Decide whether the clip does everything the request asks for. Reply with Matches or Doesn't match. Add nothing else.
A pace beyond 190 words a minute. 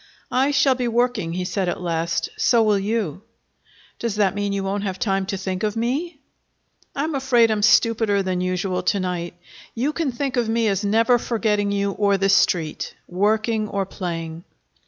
Doesn't match